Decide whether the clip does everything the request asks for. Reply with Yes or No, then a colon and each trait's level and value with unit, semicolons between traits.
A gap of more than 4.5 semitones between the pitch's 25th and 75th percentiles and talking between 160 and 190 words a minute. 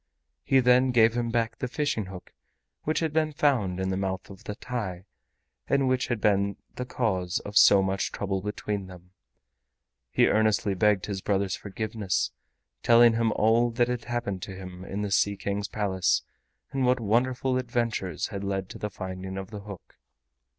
No: average, 3.9 semitones; average, 180 wpm